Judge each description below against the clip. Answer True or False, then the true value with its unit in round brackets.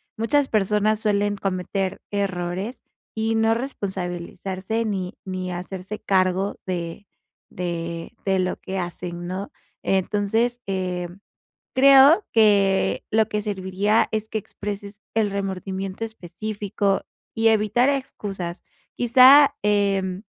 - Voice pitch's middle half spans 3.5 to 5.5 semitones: False (2.8 semitones)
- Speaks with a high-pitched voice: True (200 Hz)